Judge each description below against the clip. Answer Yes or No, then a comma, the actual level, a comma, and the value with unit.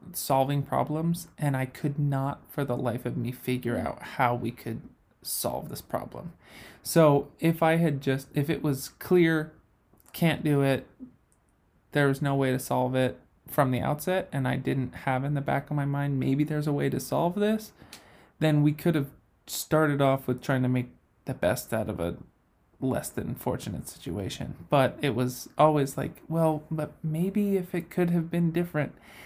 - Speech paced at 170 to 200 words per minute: Yes, average, 185 wpm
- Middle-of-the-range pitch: Yes, medium, 145 Hz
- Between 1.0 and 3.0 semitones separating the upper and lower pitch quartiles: No, average, 3.6 semitones